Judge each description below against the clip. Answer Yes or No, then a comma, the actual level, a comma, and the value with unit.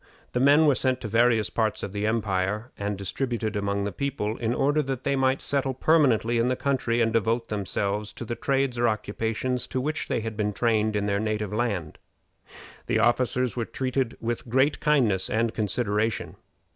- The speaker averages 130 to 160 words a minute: No, average, 185 wpm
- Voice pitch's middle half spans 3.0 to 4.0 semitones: Yes, average, 3.4 semitones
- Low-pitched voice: Yes, low, 115 Hz